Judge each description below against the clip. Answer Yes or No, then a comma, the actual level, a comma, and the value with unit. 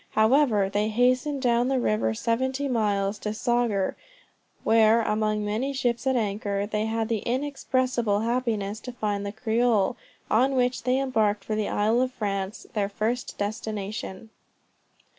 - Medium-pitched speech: No, high, 220 Hz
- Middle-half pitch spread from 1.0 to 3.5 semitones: Yes, average, 3.2 semitones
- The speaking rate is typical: Yes, average, 145 wpm